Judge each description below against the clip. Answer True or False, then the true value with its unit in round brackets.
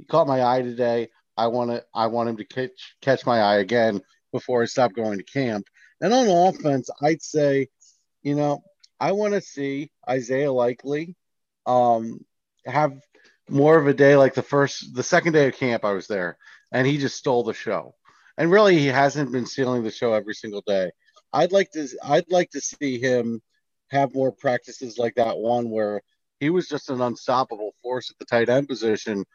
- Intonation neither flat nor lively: True (3.7 semitones)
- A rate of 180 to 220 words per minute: True (195 wpm)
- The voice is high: False (130 Hz)